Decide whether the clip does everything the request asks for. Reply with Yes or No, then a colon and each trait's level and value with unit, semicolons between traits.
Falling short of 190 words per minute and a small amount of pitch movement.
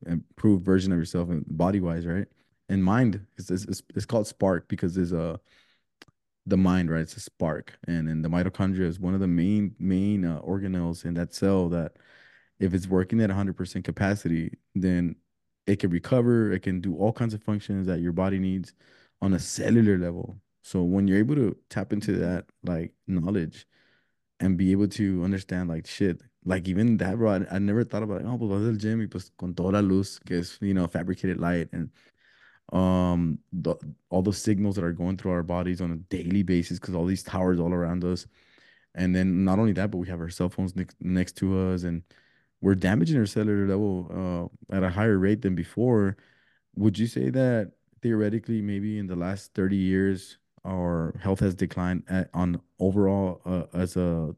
No: average, 195 wpm; narrow, 2.1 semitones